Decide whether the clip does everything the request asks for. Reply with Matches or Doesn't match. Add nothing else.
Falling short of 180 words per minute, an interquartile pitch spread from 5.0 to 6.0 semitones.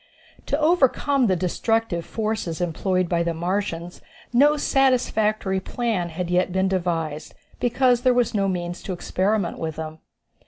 Matches